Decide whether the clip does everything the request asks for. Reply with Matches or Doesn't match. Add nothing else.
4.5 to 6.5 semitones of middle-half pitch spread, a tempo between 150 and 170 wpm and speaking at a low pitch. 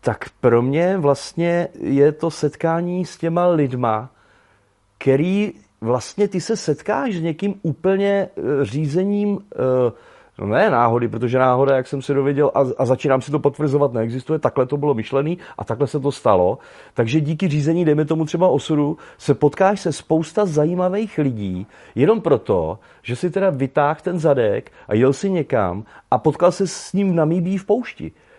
Doesn't match